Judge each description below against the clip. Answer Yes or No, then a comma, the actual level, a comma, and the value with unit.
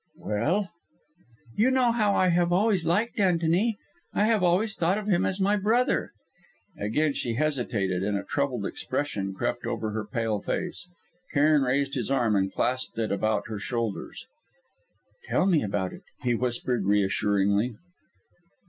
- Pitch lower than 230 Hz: Yes, low, 135 Hz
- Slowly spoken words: No, average, 155 wpm